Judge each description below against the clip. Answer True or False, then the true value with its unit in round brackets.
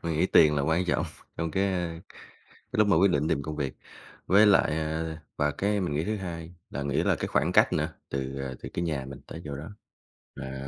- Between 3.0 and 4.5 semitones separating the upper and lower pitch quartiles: True (4.2 semitones)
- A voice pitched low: True (80 Hz)